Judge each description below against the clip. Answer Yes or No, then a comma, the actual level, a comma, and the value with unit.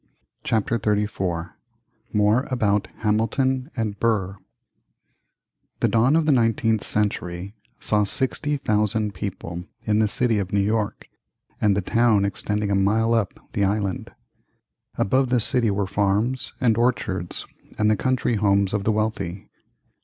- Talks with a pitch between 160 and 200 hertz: No, low, 105 Hz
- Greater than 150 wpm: No, slow, 135 wpm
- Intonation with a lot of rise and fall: No, narrow, 2.5 semitones